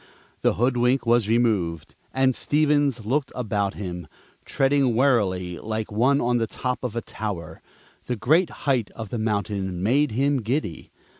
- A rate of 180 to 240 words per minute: No, average, 150 wpm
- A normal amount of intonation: Yes, average, 4.4 semitones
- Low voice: Yes, low, 120 Hz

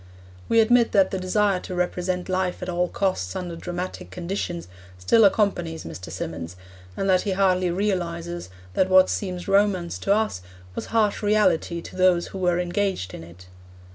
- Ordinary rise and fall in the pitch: No, narrow, 2.3 semitones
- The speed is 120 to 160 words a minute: No, average, 170 wpm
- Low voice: No, medium, 185 Hz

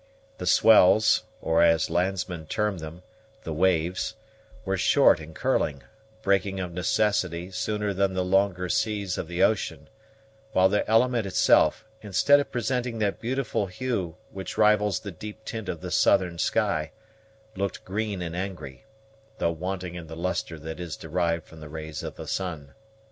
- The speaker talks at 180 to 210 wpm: No, average, 160 wpm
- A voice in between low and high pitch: No, very low, 95 Hz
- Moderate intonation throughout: Yes, average, 3.8 semitones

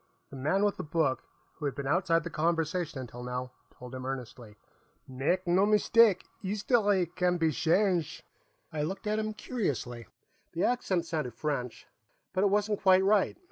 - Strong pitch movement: Yes, wide, 6.5 semitones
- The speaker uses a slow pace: No, average, 170 wpm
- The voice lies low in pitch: No, medium, 170 Hz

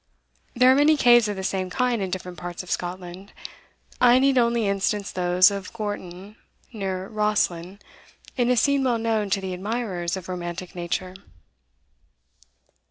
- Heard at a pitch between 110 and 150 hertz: No, high, 195 Hz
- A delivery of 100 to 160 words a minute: Yes, average, 155 wpm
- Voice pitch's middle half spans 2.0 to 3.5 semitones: No, average, 4.3 semitones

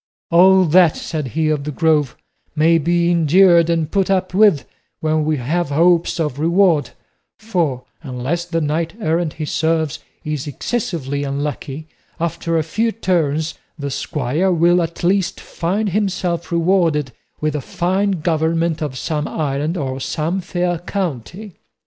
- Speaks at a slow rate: No, average, 145 wpm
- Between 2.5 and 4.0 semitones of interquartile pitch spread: Yes, average, 2.9 semitones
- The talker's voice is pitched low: No, medium, 165 Hz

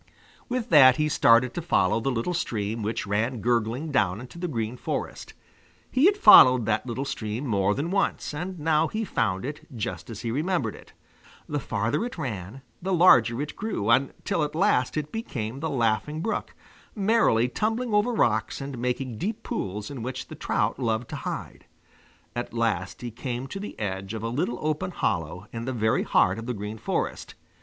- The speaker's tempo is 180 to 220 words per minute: Yes, average, 190 wpm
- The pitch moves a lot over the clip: Yes, wide, 5.8 semitones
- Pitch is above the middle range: No, low, 125 Hz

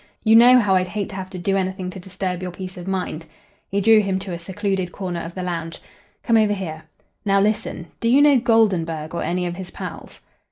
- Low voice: No, high, 190 Hz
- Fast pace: Yes, fast, 230 wpm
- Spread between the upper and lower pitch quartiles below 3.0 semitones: Yes, narrow, 2.6 semitones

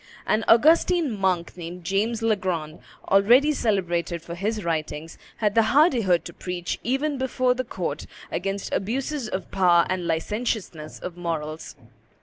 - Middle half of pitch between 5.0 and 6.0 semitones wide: Yes, wide, 5.5 semitones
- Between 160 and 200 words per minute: No, slow, 135 wpm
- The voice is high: Yes, high, 195 Hz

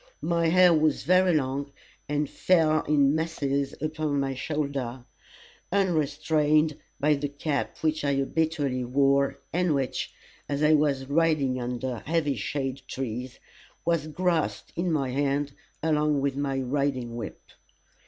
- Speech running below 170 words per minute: Yes, slow, 135 wpm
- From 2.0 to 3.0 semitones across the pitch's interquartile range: Yes, narrow, 2.5 semitones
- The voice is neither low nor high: Yes, medium, 145 Hz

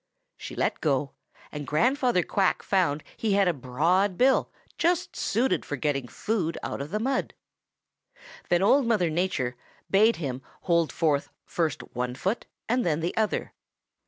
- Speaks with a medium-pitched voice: Yes, medium, 175 Hz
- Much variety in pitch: Yes, wide, 6.8 semitones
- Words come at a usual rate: Yes, average, 155 wpm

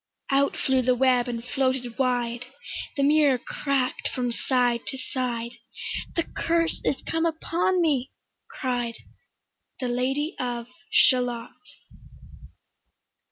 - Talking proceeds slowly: Yes, slow, 115 wpm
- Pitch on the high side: Yes, very high, 255 Hz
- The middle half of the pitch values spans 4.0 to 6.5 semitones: No, narrow, 2.4 semitones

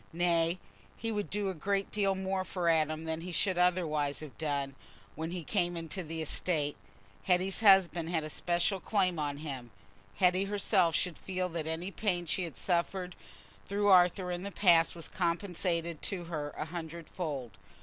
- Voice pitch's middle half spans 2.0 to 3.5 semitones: Yes, average, 2.8 semitones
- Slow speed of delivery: No, average, 170 wpm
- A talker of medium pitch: Yes, medium, 175 Hz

